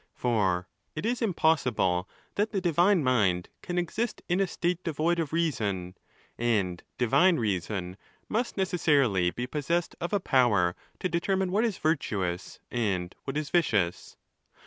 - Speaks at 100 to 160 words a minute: Yes, average, 145 wpm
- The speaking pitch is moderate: Yes, medium, 145 Hz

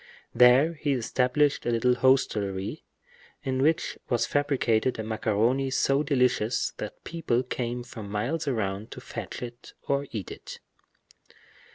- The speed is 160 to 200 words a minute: No, slow, 135 wpm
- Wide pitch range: No, average, 3.7 semitones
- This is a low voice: Yes, low, 125 Hz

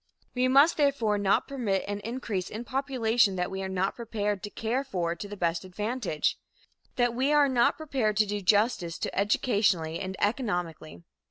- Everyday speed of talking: Yes, average, 175 wpm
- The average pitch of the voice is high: Yes, high, 210 Hz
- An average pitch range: Yes, average, 4.5 semitones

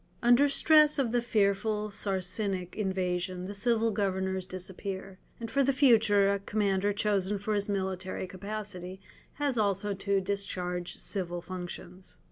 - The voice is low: No, high, 200 Hz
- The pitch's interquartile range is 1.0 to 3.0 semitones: Yes, narrow, 2.5 semitones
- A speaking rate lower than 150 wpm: Yes, slow, 135 wpm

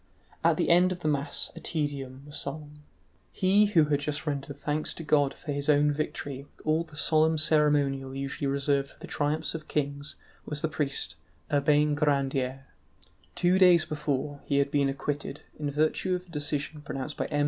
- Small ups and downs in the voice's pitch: Yes, narrow, 1.7 semitones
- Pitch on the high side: No, medium, 145 Hz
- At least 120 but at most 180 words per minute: No, average, 190 wpm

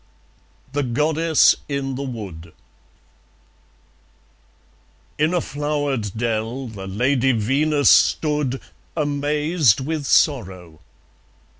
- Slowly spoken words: Yes, slow, 85 wpm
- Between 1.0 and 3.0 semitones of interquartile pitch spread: No, average, 4.8 semitones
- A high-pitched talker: No, low, 135 Hz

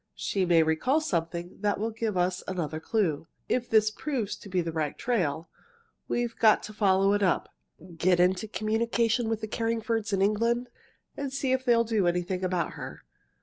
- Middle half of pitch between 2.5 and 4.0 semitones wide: No, average, 4.4 semitones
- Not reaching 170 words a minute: No, average, 185 wpm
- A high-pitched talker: Yes, high, 210 Hz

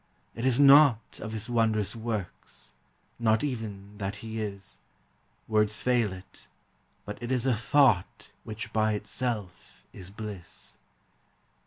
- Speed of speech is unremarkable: No, slow, 130 wpm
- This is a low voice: Yes, low, 110 Hz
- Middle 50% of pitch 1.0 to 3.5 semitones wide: Yes, narrow, 2.6 semitones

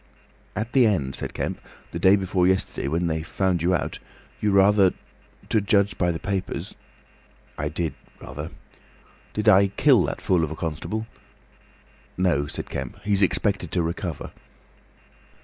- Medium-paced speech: Yes, average, 150 wpm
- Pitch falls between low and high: No, very low, 95 Hz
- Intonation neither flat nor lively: Yes, average, 3.5 semitones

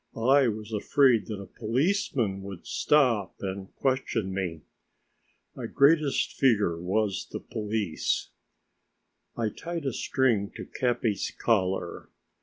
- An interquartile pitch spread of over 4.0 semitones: Yes, average, 5.1 semitones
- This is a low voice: Yes, low, 110 Hz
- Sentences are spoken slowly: Yes, slow, 115 wpm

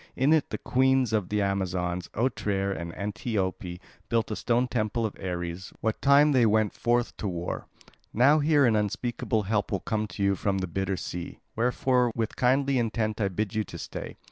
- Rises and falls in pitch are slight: No, average, 4.1 semitones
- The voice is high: No, low, 110 Hz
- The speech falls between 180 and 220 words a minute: Yes, average, 185 wpm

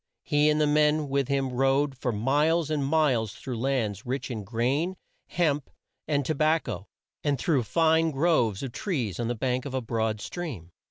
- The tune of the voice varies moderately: Yes, average, 4.1 semitones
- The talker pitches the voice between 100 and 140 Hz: Yes, low, 135 Hz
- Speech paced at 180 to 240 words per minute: Yes, average, 185 wpm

